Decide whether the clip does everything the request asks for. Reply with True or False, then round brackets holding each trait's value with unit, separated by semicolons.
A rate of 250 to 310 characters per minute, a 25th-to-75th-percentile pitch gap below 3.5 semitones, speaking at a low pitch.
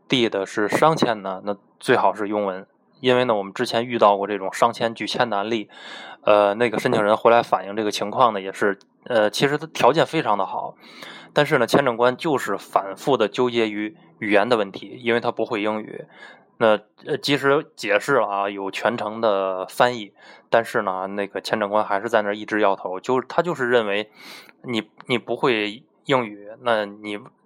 True (285 characters per minute; 3.1 semitones; 105 Hz)